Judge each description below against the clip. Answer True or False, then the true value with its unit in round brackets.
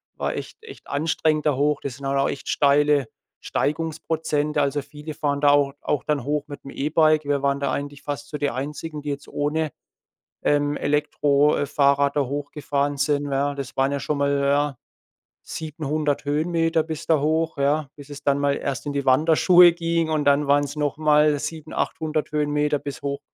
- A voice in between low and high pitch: True (145 Hz)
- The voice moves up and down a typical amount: False (1.4 semitones)